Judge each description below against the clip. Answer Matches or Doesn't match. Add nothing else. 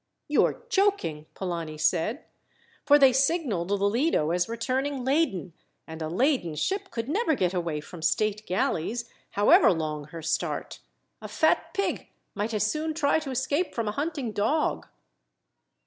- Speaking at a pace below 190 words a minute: Matches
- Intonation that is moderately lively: Doesn't match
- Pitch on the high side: Matches